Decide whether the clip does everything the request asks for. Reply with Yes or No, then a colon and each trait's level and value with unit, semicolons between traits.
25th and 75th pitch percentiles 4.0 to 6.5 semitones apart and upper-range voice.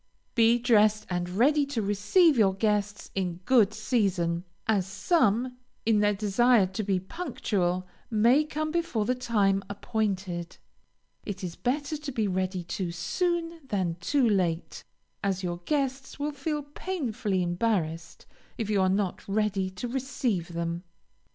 Yes: average, 5.2 semitones; high, 210 Hz